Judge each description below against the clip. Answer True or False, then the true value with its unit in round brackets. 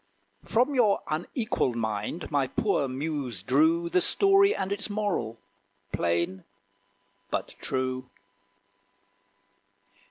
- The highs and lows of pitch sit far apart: True (8.7 semitones)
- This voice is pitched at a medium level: True (155 Hz)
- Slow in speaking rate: True (95 wpm)